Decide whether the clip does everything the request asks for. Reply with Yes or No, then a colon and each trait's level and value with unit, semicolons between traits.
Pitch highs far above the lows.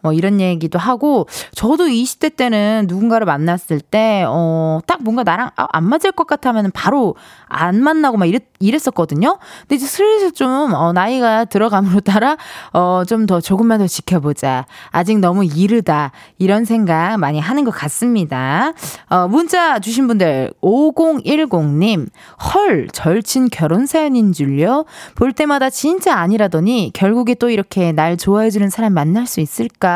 Yes: wide, 6.9 semitones